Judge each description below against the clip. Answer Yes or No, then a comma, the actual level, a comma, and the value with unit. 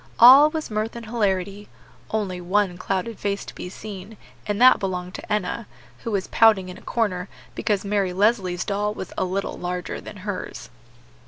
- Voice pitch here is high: Yes, high, 200 Hz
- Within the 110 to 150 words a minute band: No, average, 175 wpm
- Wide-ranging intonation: No, average, 2.9 semitones